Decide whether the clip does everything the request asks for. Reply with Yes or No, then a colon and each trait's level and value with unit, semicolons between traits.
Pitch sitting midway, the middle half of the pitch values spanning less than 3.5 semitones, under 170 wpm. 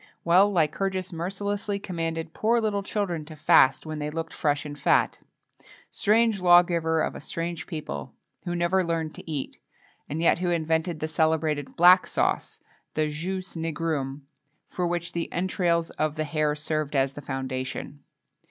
Yes: medium, 165 Hz; average, 2.7 semitones; average, 160 wpm